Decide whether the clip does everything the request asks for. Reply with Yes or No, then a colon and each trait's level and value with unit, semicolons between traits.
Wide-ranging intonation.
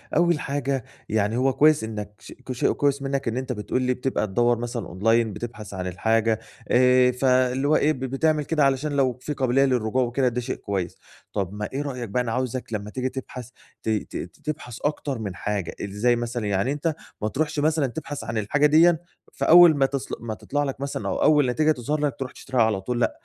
No: average, 3.9 semitones